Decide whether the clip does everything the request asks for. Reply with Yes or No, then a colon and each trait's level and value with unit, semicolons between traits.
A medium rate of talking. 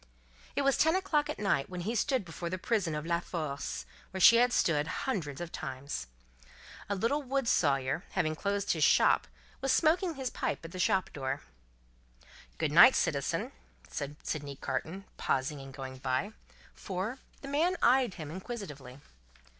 Yes: average, 165 wpm